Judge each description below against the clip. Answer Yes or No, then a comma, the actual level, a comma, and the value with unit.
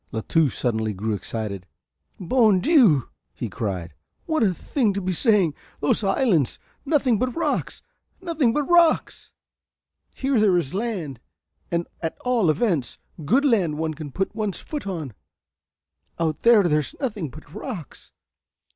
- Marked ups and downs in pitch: Yes, wide, 8.2 semitones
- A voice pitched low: No, medium, 185 Hz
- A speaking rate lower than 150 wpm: Yes, average, 140 wpm